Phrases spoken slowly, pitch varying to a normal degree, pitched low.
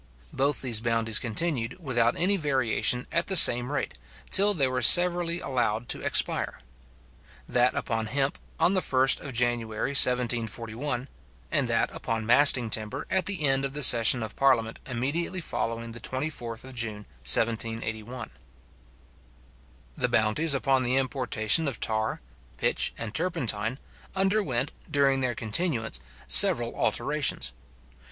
Yes: slow, 130 wpm; average, 3.9 semitones; low, 125 Hz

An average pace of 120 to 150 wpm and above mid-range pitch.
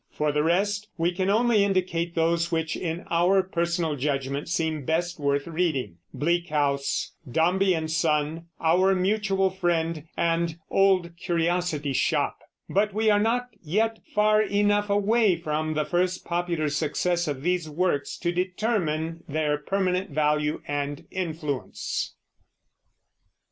No: slow, 135 wpm; medium, 170 Hz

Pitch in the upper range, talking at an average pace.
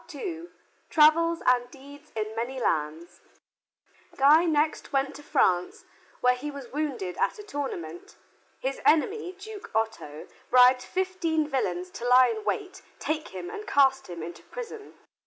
Yes: very high, 275 Hz; average, 145 wpm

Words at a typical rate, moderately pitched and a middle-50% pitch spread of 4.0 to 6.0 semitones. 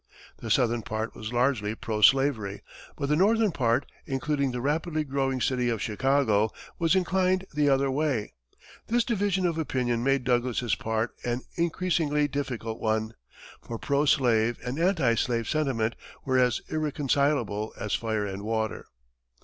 No: average, 150 wpm; low, 130 Hz; average, 4.7 semitones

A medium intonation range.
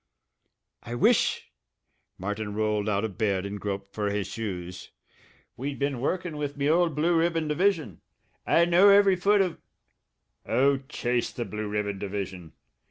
No: wide, 8.1 semitones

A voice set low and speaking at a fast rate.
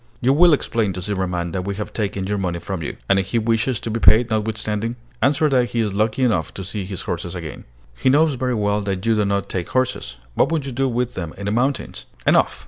Yes: low, 105 Hz; fast, 245 wpm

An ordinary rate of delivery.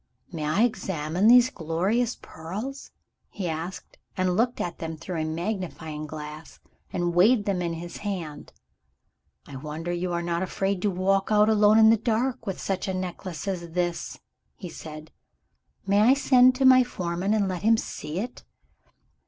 Yes: average, 170 wpm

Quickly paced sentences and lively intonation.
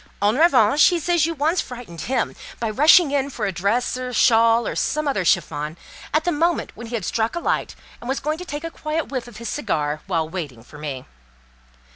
Yes: fast, 225 wpm; wide, 7.5 semitones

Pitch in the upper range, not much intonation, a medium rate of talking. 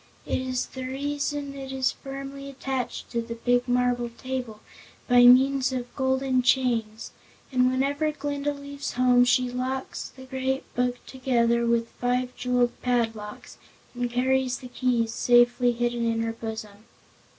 Yes: very high, 250 Hz; narrow, 1.6 semitones; average, 145 wpm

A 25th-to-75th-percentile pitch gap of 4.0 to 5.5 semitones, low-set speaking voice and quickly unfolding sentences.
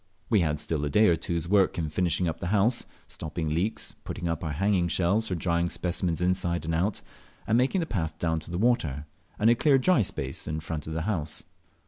Yes: average, 4.3 semitones; very low, 85 Hz; fast, 220 wpm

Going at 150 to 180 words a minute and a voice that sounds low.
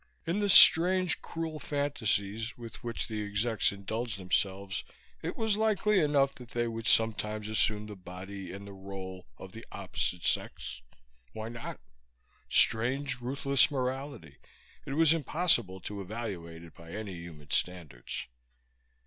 No: average, 140 wpm; low, 110 Hz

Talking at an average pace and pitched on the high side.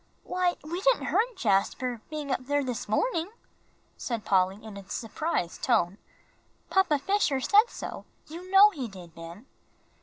Yes: average, 150 wpm; very high, 265 Hz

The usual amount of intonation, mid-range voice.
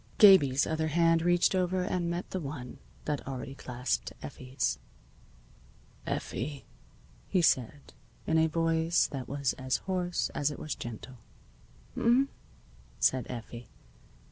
Yes: average, 4.9 semitones; medium, 155 Hz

